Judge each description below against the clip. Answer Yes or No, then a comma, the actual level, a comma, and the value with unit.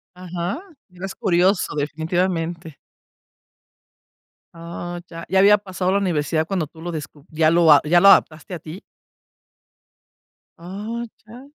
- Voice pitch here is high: No, medium, 175 Hz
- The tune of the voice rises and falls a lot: No, average, 2.9 semitones